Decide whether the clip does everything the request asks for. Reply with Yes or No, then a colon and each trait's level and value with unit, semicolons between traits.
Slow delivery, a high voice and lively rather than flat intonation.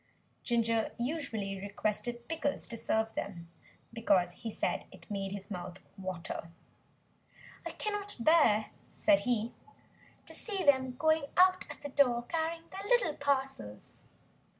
Yes: slow, 130 wpm; high, 240 Hz; wide, 7.3 semitones